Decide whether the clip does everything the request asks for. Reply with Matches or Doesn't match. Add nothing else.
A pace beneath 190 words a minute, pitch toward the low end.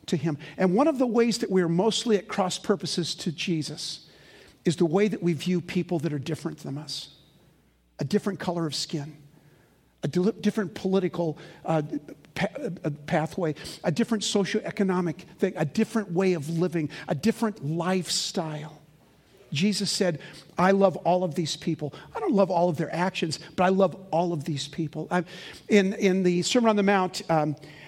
Doesn't match